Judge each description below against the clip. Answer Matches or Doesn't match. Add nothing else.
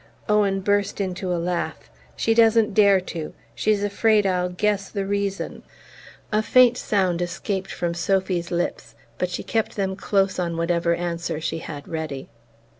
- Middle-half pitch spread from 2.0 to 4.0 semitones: Matches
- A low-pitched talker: Doesn't match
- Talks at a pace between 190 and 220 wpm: Doesn't match